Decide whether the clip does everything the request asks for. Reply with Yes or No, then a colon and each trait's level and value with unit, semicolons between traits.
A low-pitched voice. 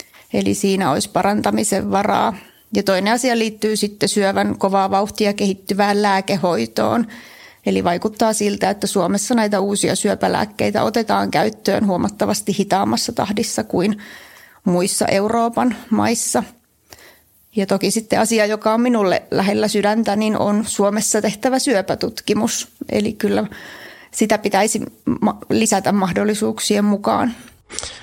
No: high, 205 Hz